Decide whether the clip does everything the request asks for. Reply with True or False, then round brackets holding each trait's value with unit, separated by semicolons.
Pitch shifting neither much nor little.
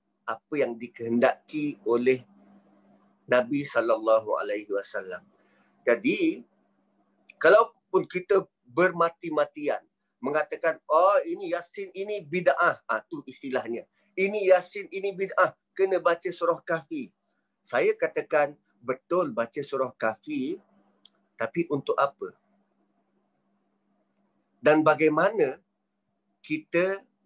False (7.5 semitones)